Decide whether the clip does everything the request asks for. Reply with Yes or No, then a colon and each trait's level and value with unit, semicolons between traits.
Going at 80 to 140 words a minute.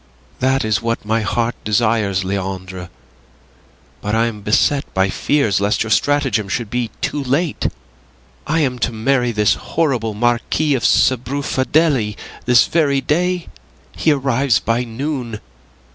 Yes: slow, 135 wpm